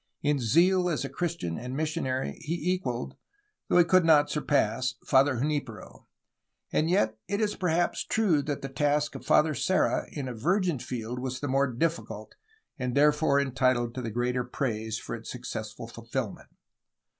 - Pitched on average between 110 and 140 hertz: Yes, low, 135 Hz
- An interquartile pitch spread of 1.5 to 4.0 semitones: No, average, 4.7 semitones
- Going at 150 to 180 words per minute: Yes, average, 165 wpm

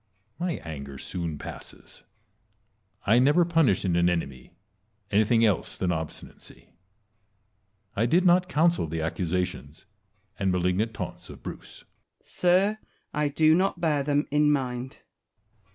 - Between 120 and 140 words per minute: Yes, slow, 135 wpm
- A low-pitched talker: Yes, low, 115 Hz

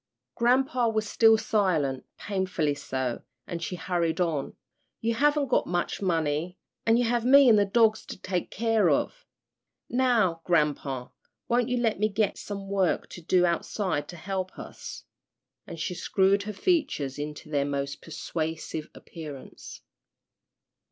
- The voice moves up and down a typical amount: No, wide, 5.9 semitones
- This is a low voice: No, medium, 185 Hz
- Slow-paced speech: No, average, 145 wpm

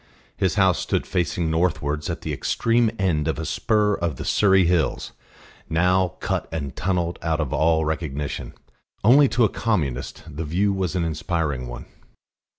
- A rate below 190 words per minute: Yes, average, 160 wpm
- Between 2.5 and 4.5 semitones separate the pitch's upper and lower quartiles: Yes, average, 3.7 semitones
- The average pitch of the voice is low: Yes, very low, 85 Hz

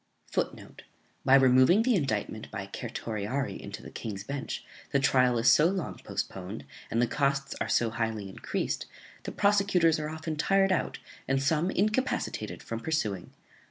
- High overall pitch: No, low, 135 Hz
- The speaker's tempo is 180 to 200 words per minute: No, average, 155 wpm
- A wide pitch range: Yes, wide, 6.4 semitones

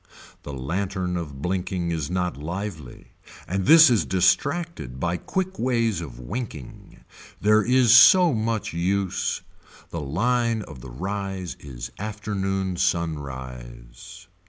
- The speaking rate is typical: No, slow, 120 wpm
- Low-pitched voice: Yes, very low, 95 Hz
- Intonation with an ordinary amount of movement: No, wide, 6.4 semitones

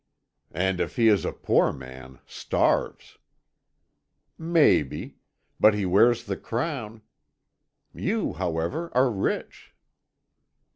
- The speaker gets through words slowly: Yes, slow, 100 wpm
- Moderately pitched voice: No, low, 105 Hz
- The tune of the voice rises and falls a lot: Yes, wide, 6.2 semitones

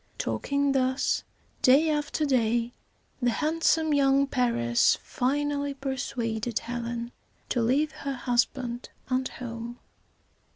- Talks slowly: Yes, slow, 100 wpm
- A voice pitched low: No, very high, 260 Hz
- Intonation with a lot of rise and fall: No, average, 2.9 semitones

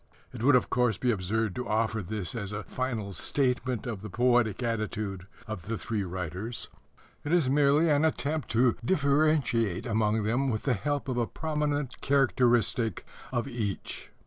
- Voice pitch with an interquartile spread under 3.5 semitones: No, average, 4.3 semitones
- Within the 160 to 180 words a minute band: Yes, average, 165 wpm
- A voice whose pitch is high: No, low, 120 Hz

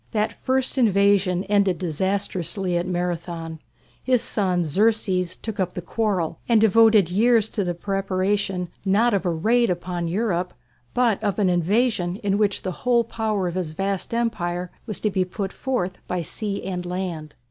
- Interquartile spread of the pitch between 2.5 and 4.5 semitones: Yes, average, 3.2 semitones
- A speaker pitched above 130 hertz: Yes, high, 190 Hz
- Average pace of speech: Yes, average, 165 wpm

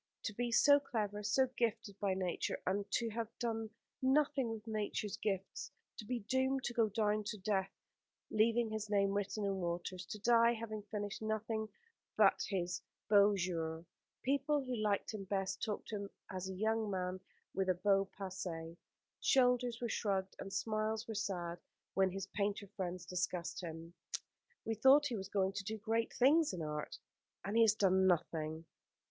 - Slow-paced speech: No, average, 175 wpm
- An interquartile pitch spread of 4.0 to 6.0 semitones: No, average, 3.1 semitones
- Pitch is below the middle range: No, high, 205 Hz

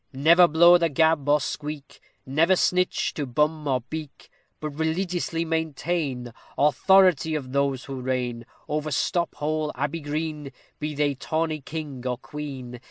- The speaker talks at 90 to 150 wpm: Yes, average, 145 wpm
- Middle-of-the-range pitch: Yes, medium, 150 Hz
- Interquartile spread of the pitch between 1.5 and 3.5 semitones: Yes, average, 2.8 semitones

